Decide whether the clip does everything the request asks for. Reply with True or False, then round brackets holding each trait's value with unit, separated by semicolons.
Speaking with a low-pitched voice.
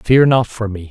True (115 Hz)